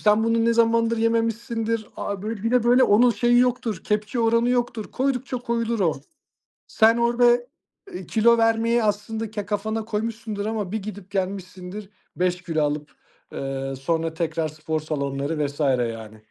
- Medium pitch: No, high, 215 Hz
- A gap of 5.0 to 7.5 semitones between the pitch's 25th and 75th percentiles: Yes, wide, 5.5 semitones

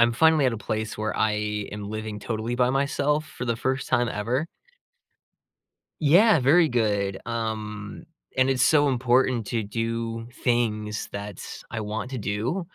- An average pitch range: Yes, average, 3.4 semitones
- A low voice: Yes, low, 115 Hz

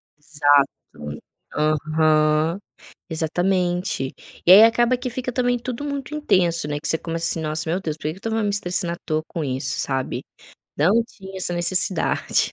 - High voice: No, medium, 170 Hz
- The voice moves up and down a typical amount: Yes, average, 5.0 semitones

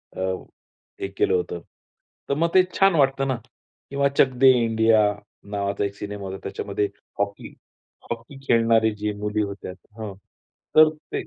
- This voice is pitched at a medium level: No, low, 110 Hz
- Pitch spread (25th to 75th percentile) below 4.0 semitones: No, average, 5.1 semitones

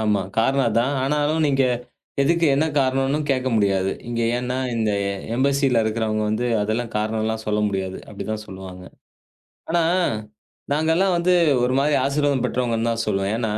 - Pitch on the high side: No, low, 120 Hz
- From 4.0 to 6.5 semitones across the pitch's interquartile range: Yes, average, 4.4 semitones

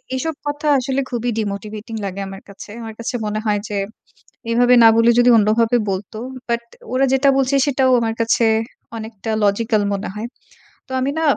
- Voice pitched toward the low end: No, high, 230 Hz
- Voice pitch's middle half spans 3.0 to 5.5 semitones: Yes, average, 3.3 semitones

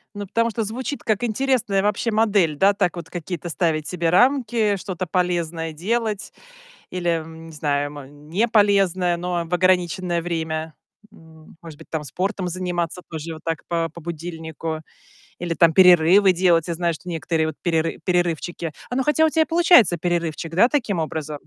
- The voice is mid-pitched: Yes, medium, 175 Hz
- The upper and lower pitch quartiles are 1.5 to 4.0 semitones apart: Yes, average, 3.7 semitones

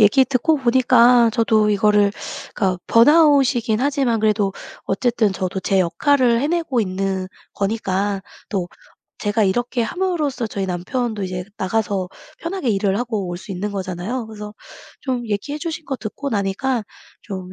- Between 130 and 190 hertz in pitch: No, high, 220 Hz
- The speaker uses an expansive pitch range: No, average, 4.7 semitones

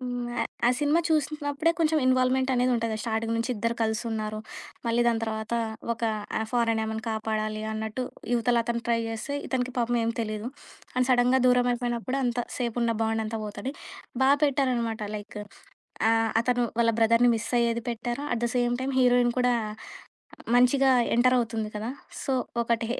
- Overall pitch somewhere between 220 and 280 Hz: Yes, high, 235 Hz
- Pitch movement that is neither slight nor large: No, narrow, 2.1 semitones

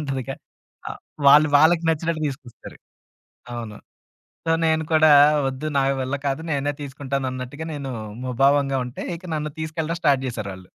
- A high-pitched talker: No, medium, 140 Hz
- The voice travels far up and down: No, average, 3.1 semitones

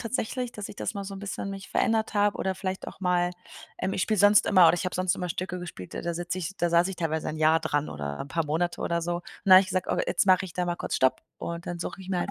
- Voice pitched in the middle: Yes, medium, 180 Hz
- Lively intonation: No, narrow, 2.4 semitones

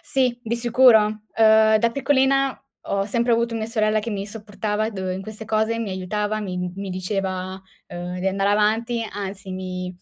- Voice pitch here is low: No, high, 210 Hz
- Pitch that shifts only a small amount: No, average, 3.2 semitones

